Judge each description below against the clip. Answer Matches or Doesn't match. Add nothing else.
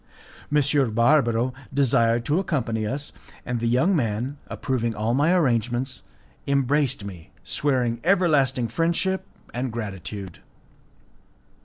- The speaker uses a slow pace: Matches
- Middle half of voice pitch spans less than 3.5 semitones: Doesn't match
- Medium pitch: Doesn't match